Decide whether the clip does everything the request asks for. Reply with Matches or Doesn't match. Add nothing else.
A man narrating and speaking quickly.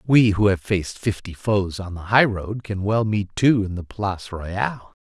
Matches